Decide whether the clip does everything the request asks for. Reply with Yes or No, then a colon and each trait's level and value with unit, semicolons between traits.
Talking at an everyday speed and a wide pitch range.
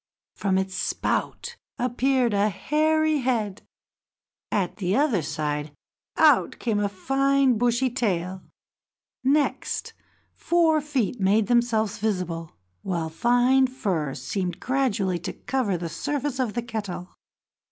No: slow, 120 wpm; wide, 5.8 semitones